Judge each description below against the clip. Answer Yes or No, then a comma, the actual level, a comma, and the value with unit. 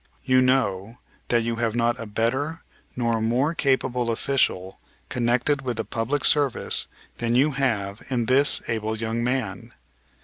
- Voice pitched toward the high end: No, low, 120 Hz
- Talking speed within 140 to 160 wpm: Yes, average, 150 wpm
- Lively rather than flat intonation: No, average, 2.7 semitones